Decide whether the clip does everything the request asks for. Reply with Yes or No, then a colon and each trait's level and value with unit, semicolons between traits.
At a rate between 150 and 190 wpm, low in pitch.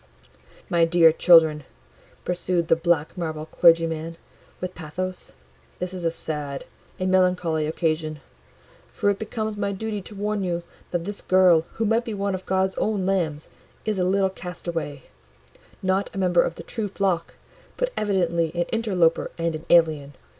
No: average, 160 wpm; medium, 180 Hz